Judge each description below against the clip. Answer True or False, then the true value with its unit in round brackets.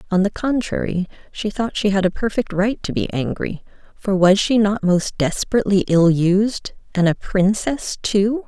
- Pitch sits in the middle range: False (200 Hz)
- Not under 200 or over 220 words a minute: False (170 wpm)